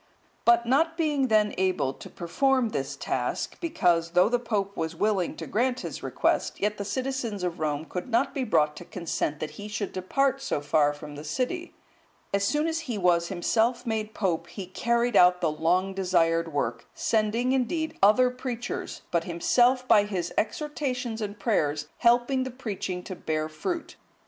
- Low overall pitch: No, high, 205 Hz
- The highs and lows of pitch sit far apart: Yes, wide, 6.6 semitones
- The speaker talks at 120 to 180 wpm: Yes, average, 175 wpm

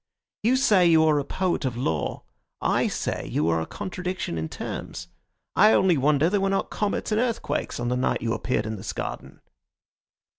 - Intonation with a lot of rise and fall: Yes, wide, 8.3 semitones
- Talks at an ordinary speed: Yes, average, 190 wpm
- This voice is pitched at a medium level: Yes, medium, 160 Hz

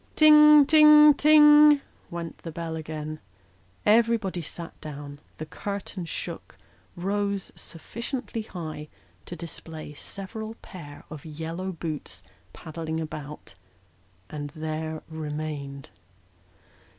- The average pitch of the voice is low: No, medium, 165 Hz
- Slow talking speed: Yes, slow, 100 wpm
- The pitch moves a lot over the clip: Yes, wide, 5.9 semitones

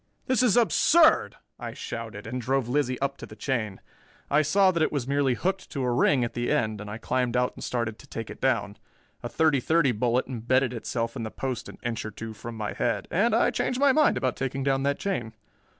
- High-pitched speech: No, low, 130 Hz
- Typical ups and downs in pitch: Yes, average, 4.2 semitones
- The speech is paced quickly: Yes, fast, 230 wpm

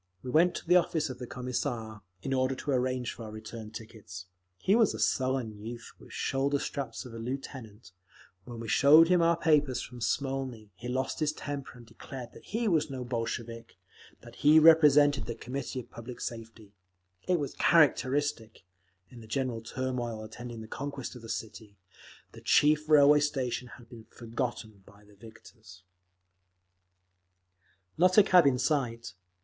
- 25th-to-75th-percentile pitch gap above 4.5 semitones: No, average, 4.1 semitones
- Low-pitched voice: Yes, low, 125 Hz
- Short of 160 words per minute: No, average, 165 wpm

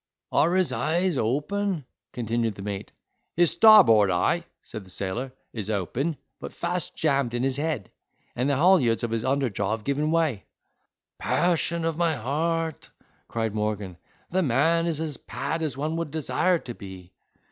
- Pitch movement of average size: No, wide, 6.7 semitones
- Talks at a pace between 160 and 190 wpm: Yes, average, 165 wpm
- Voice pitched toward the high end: No, medium, 140 Hz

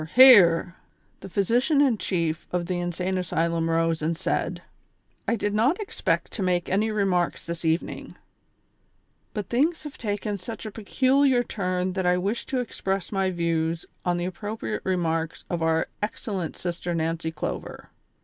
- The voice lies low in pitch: No, medium, 185 Hz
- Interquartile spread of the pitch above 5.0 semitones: No, average, 4.2 semitones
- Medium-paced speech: Yes, average, 160 wpm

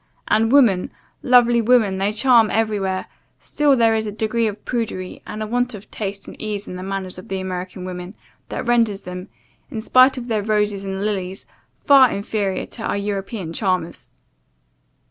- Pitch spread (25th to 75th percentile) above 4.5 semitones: No, average, 3.3 semitones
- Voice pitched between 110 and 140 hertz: No, high, 210 Hz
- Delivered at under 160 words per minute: No, average, 175 wpm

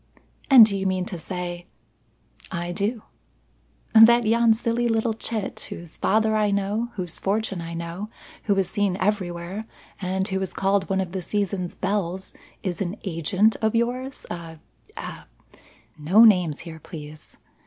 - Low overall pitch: No, high, 195 Hz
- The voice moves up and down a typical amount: Yes, average, 3.7 semitones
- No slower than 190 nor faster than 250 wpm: No, average, 165 wpm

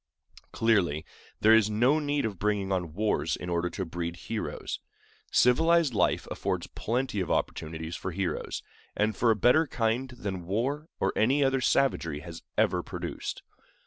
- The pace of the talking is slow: No, average, 155 wpm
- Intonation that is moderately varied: No, wide, 6.3 semitones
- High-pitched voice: No, low, 105 Hz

